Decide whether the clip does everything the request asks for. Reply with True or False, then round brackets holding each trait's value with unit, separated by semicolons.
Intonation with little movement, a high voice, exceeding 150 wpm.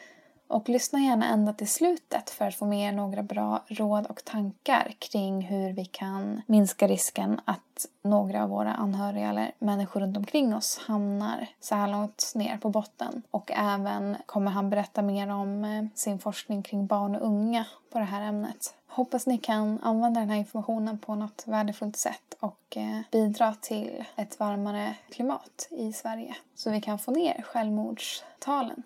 True (1.9 semitones; 210 Hz; 170 wpm)